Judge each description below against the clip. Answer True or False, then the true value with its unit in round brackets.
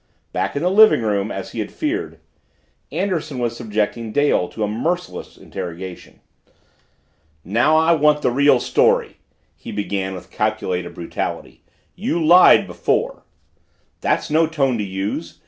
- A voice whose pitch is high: False (120 Hz)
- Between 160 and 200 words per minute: False (140 wpm)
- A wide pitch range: True (7.9 semitones)